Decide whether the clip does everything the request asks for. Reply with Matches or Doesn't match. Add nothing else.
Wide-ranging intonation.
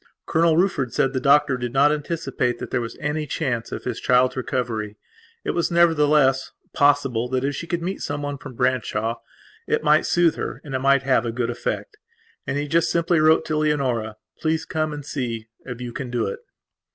Doesn't match